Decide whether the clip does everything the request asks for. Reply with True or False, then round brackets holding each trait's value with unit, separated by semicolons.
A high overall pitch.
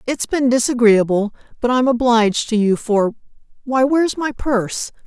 True (240 Hz)